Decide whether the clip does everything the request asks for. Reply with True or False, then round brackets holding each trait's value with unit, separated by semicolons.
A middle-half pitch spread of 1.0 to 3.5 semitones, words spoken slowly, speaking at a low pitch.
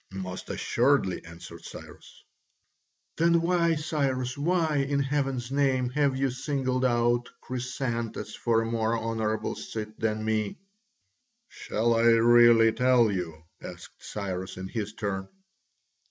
False (3.9 semitones; 125 wpm; 120 Hz)